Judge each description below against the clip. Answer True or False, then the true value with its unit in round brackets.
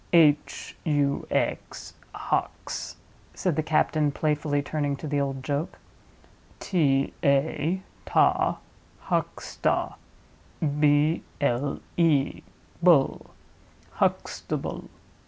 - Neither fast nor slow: False (75 wpm)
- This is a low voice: False (145 Hz)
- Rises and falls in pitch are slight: True (2.0 semitones)